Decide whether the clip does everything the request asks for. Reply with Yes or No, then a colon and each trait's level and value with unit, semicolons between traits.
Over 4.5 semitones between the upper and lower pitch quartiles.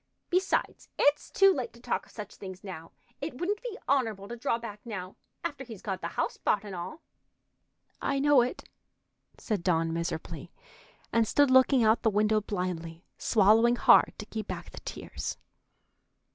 Yes: wide, 5.5 semitones